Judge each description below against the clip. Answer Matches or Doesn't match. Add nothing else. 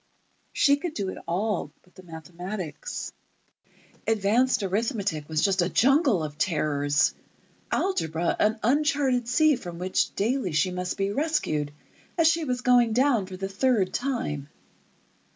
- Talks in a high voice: Matches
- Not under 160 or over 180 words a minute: Doesn't match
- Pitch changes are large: Matches